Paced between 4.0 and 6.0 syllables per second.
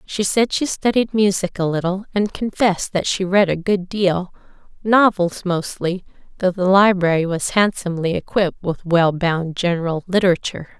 Yes: 5.0 syllables/s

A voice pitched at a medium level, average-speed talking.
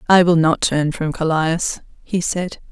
Yes: medium, 165 Hz; average, 175 wpm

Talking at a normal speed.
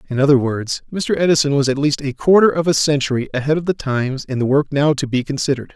No: fast, 250 wpm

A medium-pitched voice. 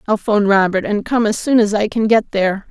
No: high, 210 Hz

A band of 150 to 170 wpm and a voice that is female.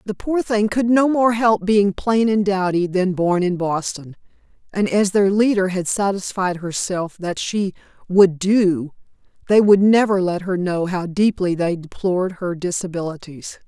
Yes: average, 165 wpm; female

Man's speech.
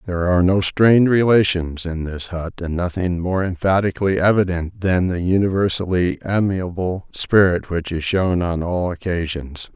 Yes: male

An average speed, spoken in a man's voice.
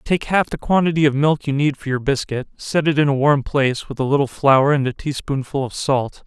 No: fast, 250 wpm; male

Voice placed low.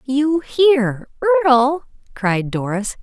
No: very high, 250 Hz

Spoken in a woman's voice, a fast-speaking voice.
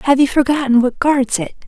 Yes: female; fast, 215 wpm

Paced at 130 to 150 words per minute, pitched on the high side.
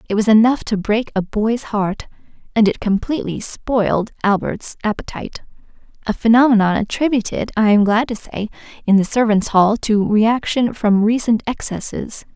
Yes: average, 145 wpm; high, 220 Hz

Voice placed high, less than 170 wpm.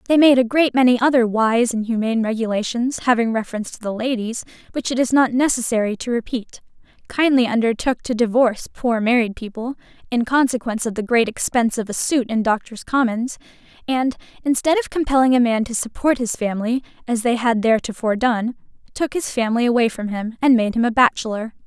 No: high, 235 Hz; average, 185 wpm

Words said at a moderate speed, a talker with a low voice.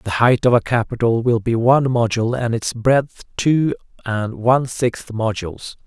Yes: average, 175 wpm; low, 120 Hz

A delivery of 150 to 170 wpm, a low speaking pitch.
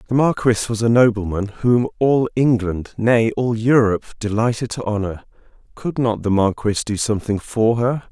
Yes: average, 165 wpm; low, 115 Hz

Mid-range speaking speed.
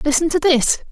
Yes: average, 195 wpm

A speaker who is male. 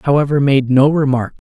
Yes: male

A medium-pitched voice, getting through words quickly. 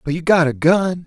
Yes: medium, 165 Hz; fast, 280 wpm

